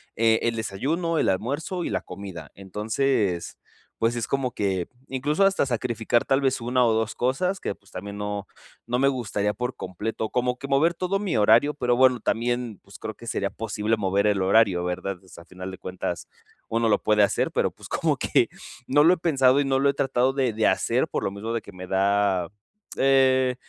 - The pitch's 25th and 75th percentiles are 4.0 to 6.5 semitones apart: Yes, average, 4.8 semitones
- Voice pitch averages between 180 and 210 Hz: No, low, 115 Hz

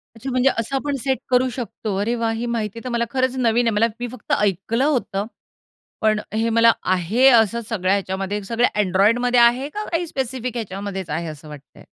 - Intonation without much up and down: No, average, 3.6 semitones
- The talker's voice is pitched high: Yes, high, 230 Hz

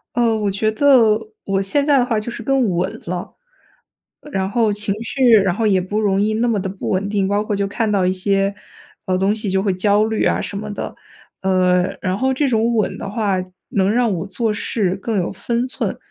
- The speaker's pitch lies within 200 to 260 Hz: Yes, high, 205 Hz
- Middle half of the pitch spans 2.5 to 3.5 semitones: Yes, average, 2.8 semitones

